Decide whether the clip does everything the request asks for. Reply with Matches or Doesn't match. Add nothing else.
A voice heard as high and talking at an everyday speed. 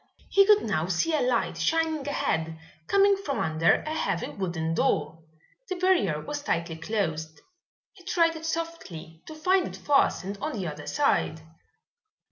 Matches